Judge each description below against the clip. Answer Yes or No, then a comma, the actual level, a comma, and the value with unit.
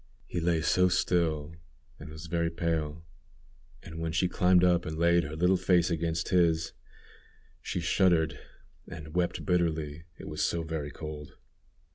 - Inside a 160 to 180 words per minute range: No, average, 150 wpm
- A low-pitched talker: Yes, very low, 85 Hz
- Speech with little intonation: Yes, narrow, 1.7 semitones